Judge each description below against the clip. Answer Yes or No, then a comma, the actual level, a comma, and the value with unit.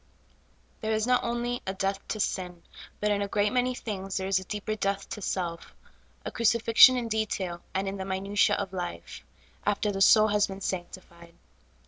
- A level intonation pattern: Yes, narrow, 2.3 semitones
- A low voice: No, high, 200 Hz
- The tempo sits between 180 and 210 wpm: Yes, average, 195 wpm